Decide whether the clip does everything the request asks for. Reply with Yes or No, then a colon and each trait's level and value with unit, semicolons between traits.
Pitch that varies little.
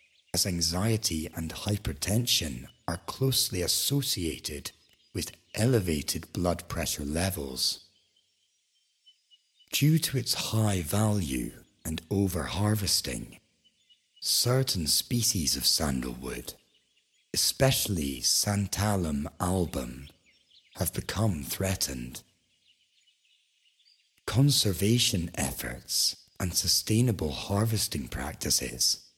No: wide, 5.5 semitones